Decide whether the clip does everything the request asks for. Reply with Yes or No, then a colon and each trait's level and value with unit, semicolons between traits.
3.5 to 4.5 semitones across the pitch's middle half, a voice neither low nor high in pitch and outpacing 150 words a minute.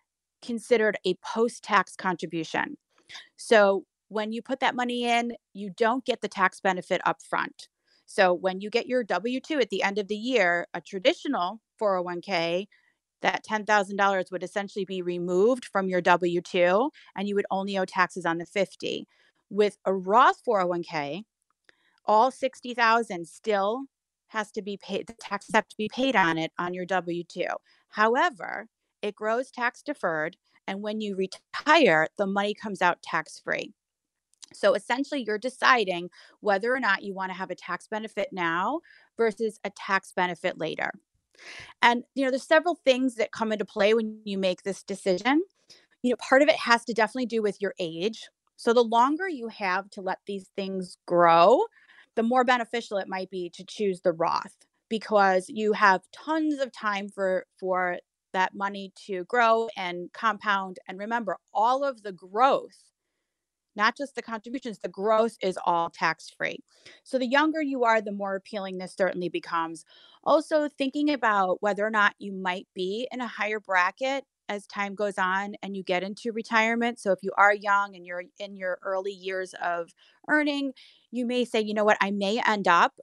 No: average, 4.2 semitones; high, 205 Hz; average, 175 wpm